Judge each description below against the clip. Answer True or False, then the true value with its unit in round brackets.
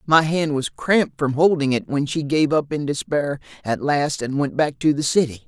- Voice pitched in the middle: True (145 Hz)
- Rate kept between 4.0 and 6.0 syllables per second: True (5.0 syllables/s)